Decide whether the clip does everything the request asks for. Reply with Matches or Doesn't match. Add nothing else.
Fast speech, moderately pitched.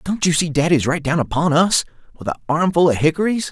Matches